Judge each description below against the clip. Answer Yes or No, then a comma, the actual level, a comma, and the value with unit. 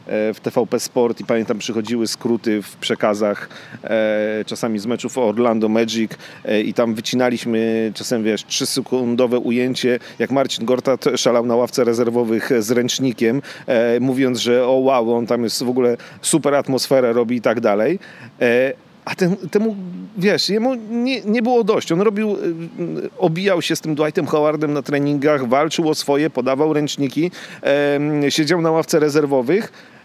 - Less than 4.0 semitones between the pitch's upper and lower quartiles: No, average, 4.7 semitones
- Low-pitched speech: Yes, low, 130 Hz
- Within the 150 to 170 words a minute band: Yes, fast, 160 wpm